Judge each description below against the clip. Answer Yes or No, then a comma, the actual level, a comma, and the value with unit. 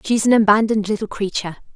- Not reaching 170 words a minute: No, fast, 205 wpm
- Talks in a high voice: Yes, high, 210 Hz